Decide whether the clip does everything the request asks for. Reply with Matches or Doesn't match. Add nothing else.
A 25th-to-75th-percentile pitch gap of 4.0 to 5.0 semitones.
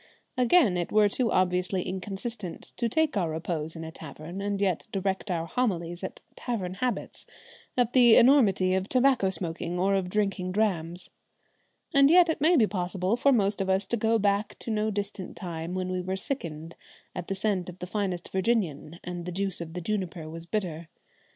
Doesn't match